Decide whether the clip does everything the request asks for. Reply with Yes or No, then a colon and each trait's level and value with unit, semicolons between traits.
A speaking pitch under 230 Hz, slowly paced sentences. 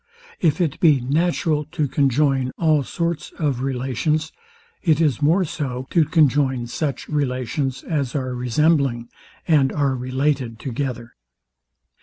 Yes: medium, 140 Hz; slow, 125 wpm